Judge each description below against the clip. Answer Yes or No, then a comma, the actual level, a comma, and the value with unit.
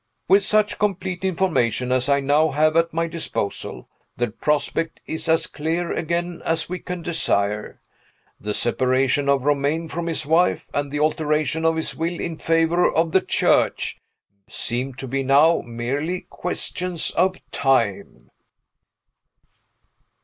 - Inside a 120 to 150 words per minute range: Yes, average, 140 wpm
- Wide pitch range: No, average, 3.7 semitones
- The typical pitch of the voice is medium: Yes, medium, 160 Hz